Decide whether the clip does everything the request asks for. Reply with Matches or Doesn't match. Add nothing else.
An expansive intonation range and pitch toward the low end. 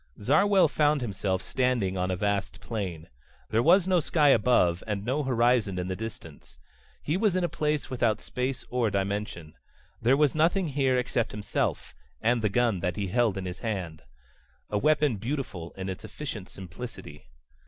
Matches